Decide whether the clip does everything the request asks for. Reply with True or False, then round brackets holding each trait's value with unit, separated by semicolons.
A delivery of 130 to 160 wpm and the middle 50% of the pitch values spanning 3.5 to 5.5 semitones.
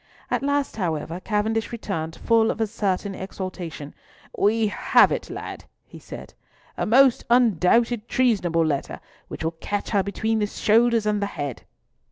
True (145 wpm; 4.1 semitones)